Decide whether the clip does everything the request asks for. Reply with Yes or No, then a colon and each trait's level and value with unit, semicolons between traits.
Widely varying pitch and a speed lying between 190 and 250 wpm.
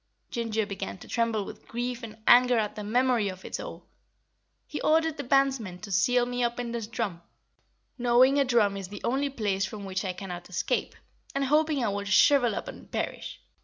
No: average, 3.8 semitones; average, 200 wpm